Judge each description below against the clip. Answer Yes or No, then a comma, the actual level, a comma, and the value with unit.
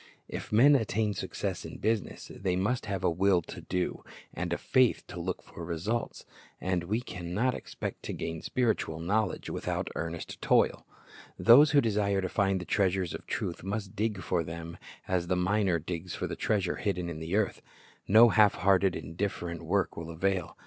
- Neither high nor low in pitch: No, very low, 95 Hz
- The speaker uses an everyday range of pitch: Yes, average, 3.6 semitones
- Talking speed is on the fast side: No, average, 185 wpm